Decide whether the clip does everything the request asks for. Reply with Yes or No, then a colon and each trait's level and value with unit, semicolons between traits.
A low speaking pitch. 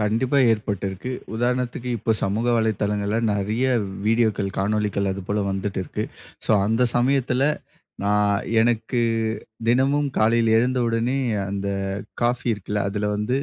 Yes: low, 110 Hz